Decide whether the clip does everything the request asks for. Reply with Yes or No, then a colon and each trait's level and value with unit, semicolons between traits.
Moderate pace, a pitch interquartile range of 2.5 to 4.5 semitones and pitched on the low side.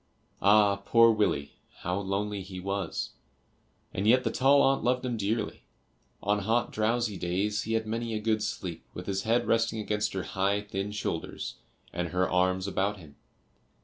Yes: average, 170 wpm; average, 2.9 semitones; low, 105 Hz